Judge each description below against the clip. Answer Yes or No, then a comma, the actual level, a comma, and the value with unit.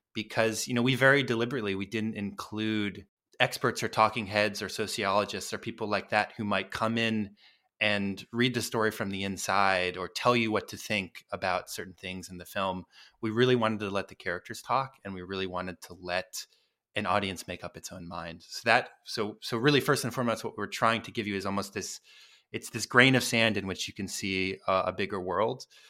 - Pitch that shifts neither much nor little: Yes, average, 3.1 semitones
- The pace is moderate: No, fast, 220 wpm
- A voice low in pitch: Yes, low, 105 Hz